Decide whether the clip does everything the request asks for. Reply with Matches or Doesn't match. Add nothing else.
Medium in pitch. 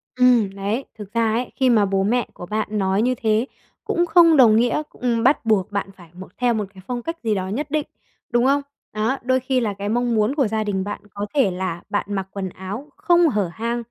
Doesn't match